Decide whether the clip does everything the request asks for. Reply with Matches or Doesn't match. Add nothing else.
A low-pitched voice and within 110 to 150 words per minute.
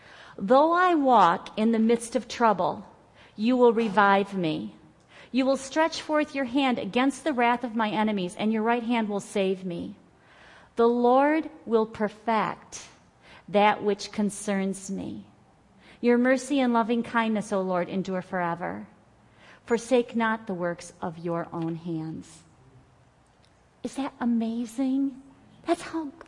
Doesn't match